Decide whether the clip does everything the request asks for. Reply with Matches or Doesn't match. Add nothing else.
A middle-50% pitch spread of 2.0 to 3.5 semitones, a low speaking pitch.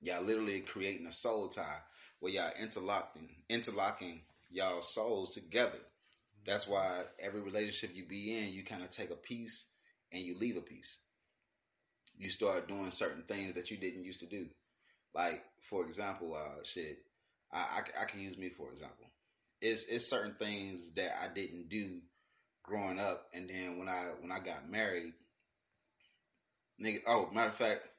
Matches